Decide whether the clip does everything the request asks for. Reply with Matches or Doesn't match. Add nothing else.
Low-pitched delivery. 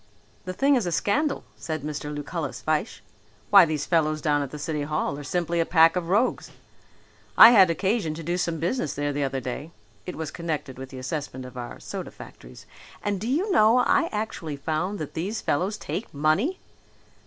Doesn't match